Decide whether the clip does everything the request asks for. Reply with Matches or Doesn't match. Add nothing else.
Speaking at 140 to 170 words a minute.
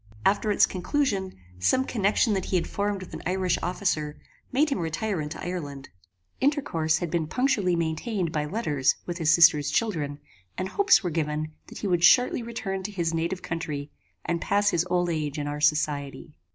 Doesn't match